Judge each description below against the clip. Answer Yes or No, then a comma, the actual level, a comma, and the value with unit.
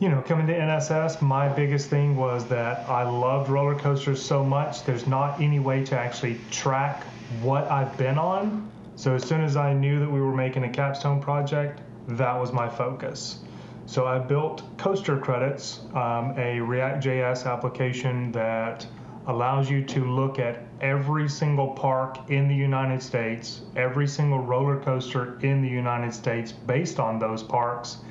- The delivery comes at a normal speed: Yes, average, 165 wpm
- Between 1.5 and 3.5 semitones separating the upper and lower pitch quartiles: Yes, narrow, 2.6 semitones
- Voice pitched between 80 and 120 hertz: No, low, 130 Hz